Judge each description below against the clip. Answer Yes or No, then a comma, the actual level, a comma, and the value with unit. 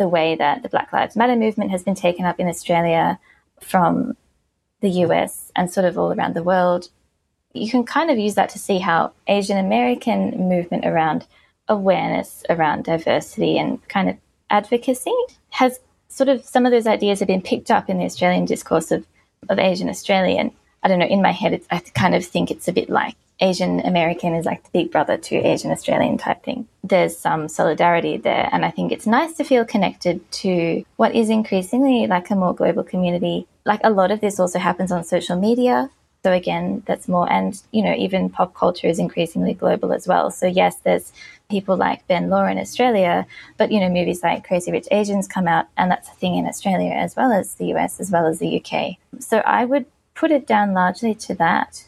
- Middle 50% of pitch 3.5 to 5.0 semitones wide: Yes, average, 4.3 semitones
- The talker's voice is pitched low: No, high, 195 Hz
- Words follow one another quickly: Yes, fast, 210 wpm